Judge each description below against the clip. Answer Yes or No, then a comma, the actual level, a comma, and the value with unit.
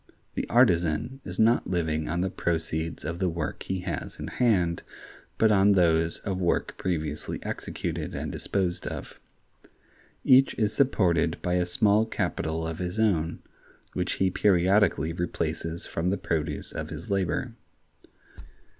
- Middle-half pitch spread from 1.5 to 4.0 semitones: Yes, average, 3.3 semitones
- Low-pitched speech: Yes, very low, 90 Hz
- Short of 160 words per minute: Yes, average, 145 wpm